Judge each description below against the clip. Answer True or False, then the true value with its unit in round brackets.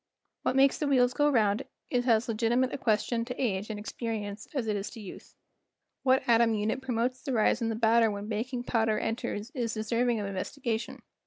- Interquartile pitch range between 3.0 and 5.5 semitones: False (2.5 semitones)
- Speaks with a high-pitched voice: True (230 Hz)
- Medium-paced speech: False (210 wpm)